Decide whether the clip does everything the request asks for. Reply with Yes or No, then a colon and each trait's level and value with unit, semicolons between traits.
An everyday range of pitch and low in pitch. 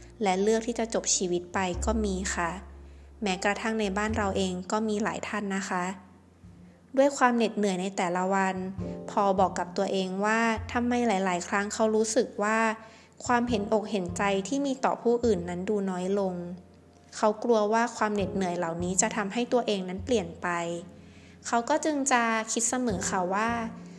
No: average, 3.4 semitones; high, 205 Hz